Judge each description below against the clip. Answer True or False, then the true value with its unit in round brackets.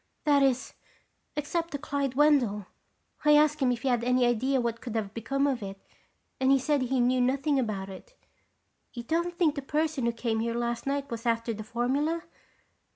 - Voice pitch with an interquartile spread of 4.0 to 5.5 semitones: False (3.5 semitones)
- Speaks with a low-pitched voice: False (260 Hz)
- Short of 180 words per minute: False (195 wpm)